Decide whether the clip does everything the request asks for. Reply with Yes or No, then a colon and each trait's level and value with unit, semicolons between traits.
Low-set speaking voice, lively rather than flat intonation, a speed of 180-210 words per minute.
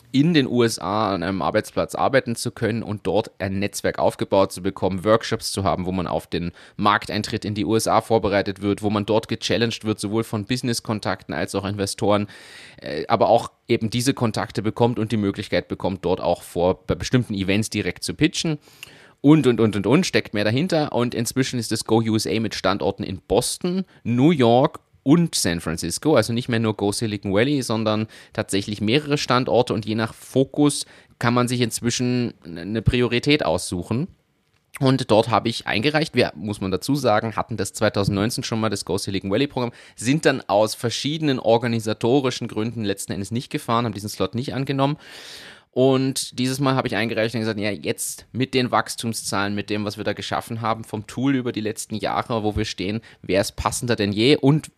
No: low, 115 Hz; average, 3.4 semitones; fast, 190 wpm